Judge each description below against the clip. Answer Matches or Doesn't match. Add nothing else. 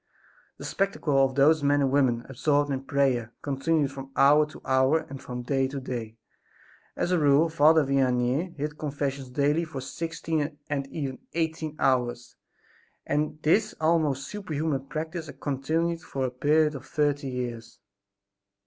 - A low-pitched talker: Doesn't match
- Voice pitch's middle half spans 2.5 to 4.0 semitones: Matches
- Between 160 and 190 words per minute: Doesn't match